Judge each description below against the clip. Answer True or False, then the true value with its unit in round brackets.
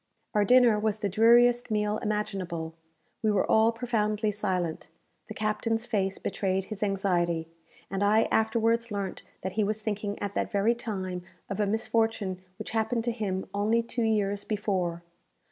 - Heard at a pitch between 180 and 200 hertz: False (210 Hz)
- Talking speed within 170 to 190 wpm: False (160 wpm)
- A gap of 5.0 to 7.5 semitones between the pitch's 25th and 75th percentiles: False (2.4 semitones)